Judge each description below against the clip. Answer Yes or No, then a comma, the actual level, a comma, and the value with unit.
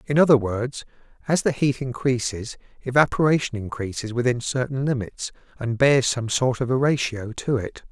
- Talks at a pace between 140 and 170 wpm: Yes, average, 160 wpm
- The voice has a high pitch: No, low, 125 Hz